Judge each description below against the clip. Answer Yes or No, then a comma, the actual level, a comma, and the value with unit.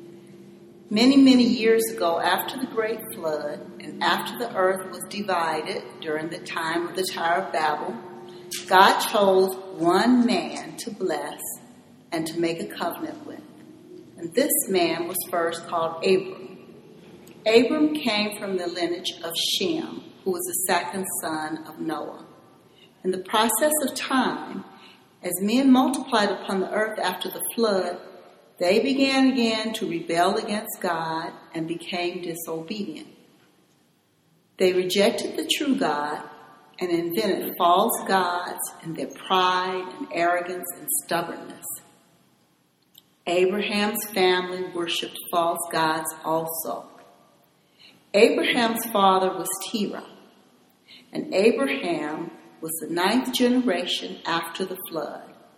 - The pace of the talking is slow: Yes, slow, 125 wpm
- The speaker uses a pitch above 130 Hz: Yes, medium, 185 Hz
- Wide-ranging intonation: No, average, 4.3 semitones